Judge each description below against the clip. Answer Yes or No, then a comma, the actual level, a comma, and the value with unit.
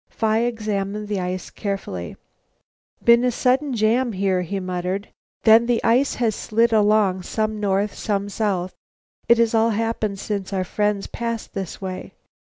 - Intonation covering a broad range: No, average, 2.8 semitones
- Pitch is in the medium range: No, high, 210 Hz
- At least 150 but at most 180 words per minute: Yes, average, 155 wpm